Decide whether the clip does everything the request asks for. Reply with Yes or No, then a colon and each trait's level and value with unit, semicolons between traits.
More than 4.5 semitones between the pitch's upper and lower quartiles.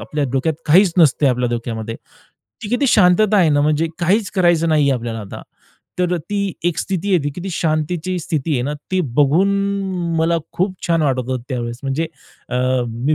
Yes: average, 5.1 semitones